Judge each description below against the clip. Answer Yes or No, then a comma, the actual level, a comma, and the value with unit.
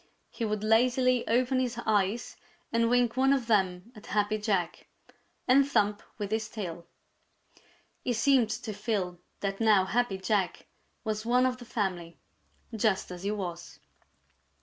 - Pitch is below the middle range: No, high, 215 Hz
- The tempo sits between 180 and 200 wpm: No, average, 150 wpm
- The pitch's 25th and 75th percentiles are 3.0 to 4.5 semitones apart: Yes, average, 3.7 semitones